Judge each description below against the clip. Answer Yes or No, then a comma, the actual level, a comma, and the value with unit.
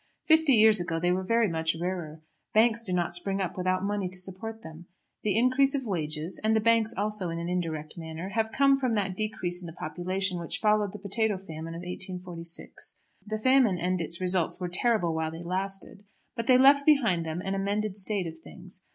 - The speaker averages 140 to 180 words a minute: No, fast, 205 wpm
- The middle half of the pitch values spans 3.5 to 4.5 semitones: Yes, average, 4.0 semitones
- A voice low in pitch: No, medium, 185 Hz